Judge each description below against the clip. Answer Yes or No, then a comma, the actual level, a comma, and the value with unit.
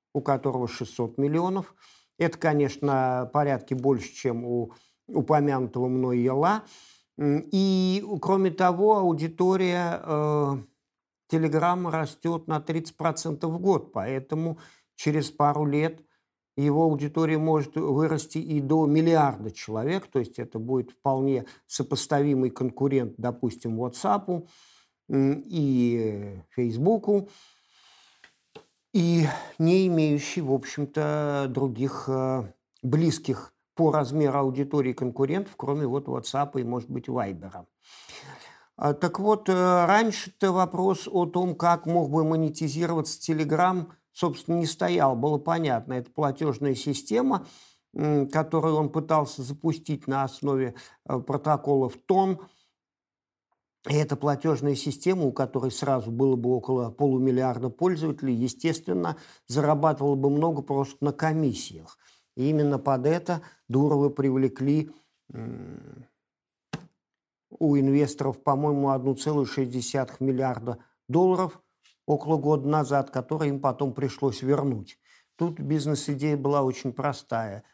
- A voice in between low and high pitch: Yes, medium, 145 Hz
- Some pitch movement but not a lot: Yes, average, 3.4 semitones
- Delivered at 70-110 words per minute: Yes, average, 105 wpm